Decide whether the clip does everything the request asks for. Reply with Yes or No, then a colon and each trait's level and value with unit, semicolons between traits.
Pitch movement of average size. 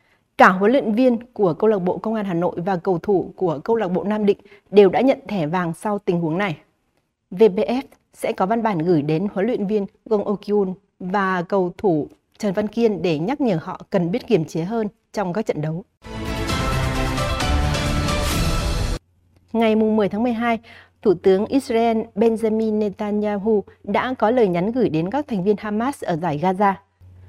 Yes: average, 4.5 semitones